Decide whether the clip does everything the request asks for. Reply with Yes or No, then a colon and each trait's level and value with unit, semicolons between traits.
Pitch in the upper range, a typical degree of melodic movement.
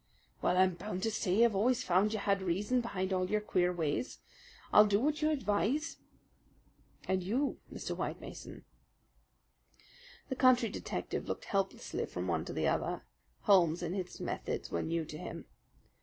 Yes: high, 195 Hz; average, 4.2 semitones